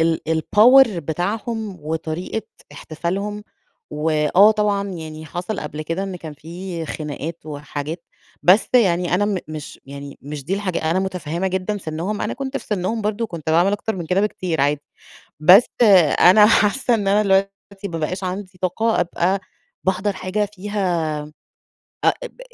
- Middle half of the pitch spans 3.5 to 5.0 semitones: Yes, average, 4.3 semitones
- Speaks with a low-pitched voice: No, medium, 185 Hz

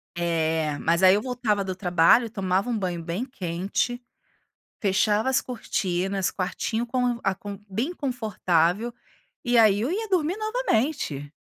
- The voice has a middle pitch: No, high, 205 Hz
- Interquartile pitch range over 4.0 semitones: Yes, wide, 5.4 semitones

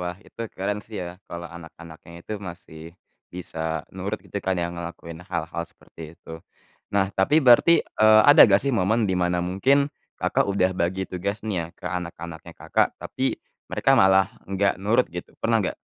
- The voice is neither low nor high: No, very low, 95 Hz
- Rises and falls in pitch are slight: No, average, 3.4 semitones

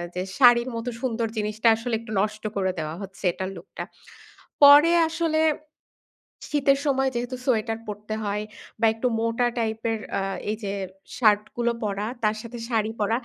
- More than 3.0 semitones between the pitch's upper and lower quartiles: No, average, 2.7 semitones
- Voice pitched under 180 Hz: No, high, 225 Hz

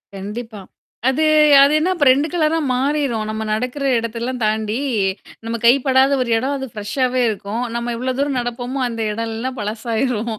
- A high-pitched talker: Yes, high, 245 Hz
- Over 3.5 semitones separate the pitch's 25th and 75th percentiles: No, average, 3.1 semitones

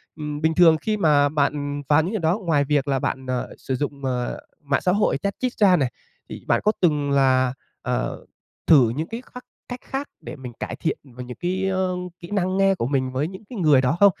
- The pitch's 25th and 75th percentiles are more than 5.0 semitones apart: Yes, wide, 5.6 semitones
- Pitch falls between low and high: Yes, medium, 150 Hz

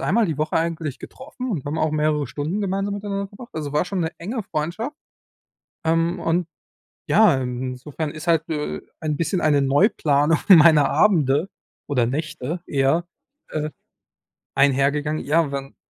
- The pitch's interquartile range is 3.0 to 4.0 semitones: Yes, average, 3.6 semitones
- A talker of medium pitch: Yes, medium, 155 Hz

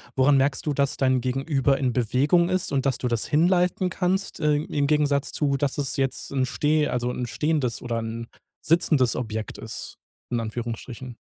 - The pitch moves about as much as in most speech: Yes, average, 3.2 semitones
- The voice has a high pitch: No, low, 135 Hz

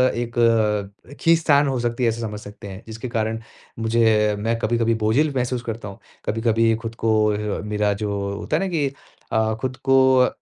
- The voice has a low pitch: Yes, low, 115 Hz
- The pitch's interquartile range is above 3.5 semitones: No, average, 2.7 semitones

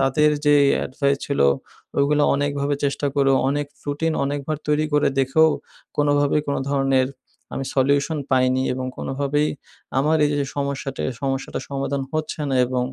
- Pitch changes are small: Yes, narrow, 1.4 semitones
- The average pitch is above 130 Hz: Yes, medium, 140 Hz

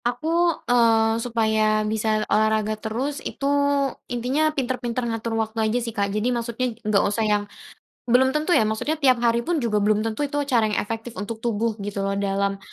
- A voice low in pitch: No, high, 225 Hz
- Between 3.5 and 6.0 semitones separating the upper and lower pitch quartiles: No, narrow, 2.4 semitones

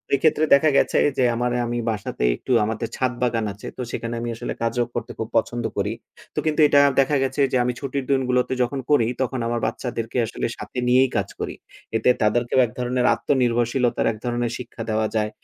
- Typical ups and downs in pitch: No, narrow, 2.1 semitones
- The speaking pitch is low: Yes, low, 120 Hz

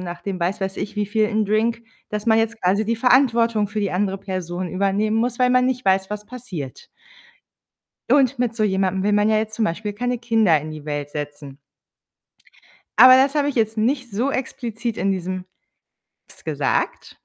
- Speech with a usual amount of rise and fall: Yes, average, 3.6 semitones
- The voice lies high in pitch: Yes, high, 215 Hz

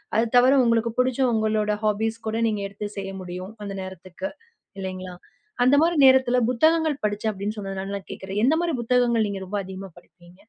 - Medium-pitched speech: No, high, 210 Hz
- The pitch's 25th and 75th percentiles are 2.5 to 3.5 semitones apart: No, average, 4.2 semitones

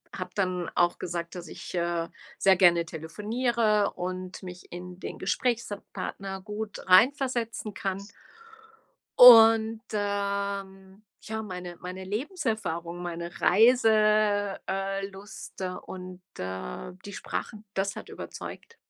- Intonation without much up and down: No, average, 3.4 semitones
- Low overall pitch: No, high, 195 Hz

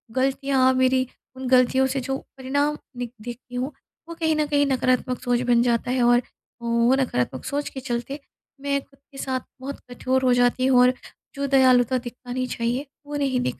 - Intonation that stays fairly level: Yes, narrow, 1.7 semitones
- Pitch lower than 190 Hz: No, very high, 255 Hz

